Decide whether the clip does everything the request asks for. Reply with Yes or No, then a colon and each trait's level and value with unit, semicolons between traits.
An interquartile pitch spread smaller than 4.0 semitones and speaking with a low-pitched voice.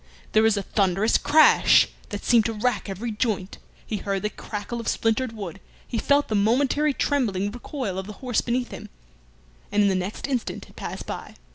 No: average, 3.5 semitones; high, 220 Hz